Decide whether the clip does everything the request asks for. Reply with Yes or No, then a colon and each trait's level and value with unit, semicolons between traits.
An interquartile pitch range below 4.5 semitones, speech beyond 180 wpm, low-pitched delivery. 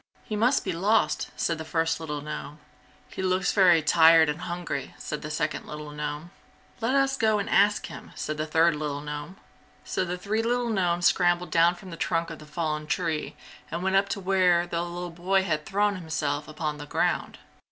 No: average, 3.7 semitones; average, 200 wpm; medium, 170 Hz